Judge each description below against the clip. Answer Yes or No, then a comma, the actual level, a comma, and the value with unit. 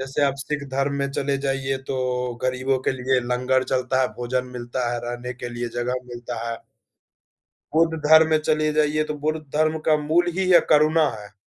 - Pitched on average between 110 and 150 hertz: Yes, low, 135 Hz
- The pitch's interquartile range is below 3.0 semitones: No, average, 3.4 semitones